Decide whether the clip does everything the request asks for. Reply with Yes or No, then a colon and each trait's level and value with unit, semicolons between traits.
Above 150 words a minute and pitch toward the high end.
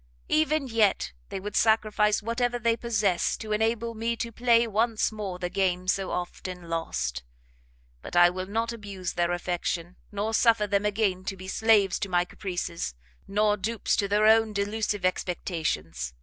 Yes: average, 165 wpm; high, 205 Hz